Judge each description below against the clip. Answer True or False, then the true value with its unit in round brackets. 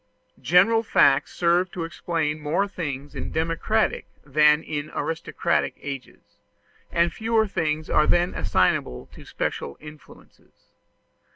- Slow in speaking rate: True (115 wpm)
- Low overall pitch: False (160 Hz)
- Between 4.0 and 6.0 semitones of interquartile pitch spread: False (2.8 semitones)